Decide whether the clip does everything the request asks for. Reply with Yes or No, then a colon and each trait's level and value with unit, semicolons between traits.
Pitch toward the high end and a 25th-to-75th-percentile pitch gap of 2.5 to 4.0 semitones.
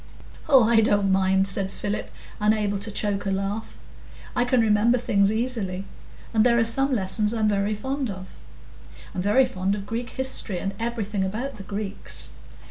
Yes: high, 210 Hz; average, 3.0 semitones